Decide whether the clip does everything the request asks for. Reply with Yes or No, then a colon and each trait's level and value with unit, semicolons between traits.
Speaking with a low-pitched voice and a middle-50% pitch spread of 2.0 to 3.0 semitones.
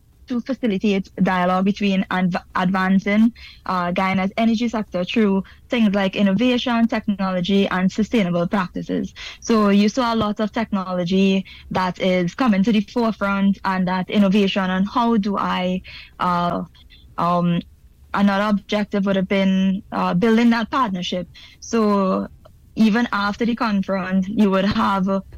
No: high, 195 Hz; average, 2.7 semitones